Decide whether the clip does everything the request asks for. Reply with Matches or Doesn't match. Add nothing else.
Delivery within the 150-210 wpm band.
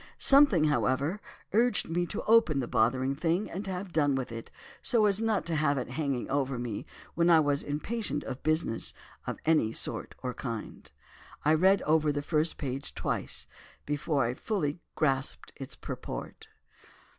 Matches